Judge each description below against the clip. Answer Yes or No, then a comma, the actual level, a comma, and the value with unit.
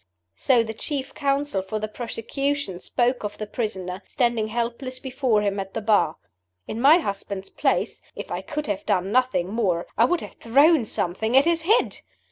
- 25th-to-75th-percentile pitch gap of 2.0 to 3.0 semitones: No, average, 4.9 semitones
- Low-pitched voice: No, high, 230 Hz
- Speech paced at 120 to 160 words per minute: No, average, 180 wpm